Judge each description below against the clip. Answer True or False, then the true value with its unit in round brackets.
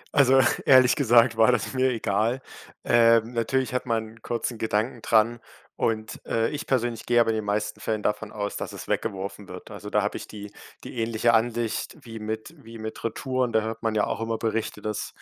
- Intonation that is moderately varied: False (1.7 semitones)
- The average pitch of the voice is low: True (115 Hz)